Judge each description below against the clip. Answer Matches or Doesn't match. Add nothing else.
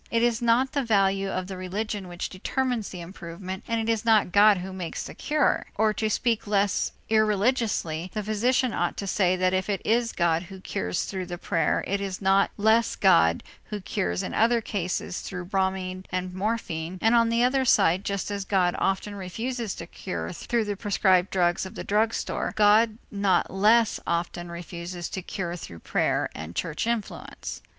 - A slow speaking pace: Doesn't match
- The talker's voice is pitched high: Matches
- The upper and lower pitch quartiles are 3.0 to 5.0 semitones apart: Matches